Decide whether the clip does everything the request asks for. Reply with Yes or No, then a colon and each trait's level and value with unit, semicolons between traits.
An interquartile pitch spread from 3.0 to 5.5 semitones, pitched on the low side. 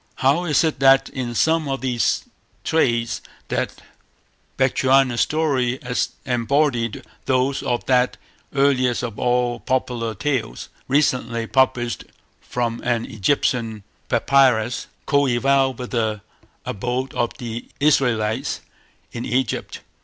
No: narrow, 2.5 semitones; low, 125 Hz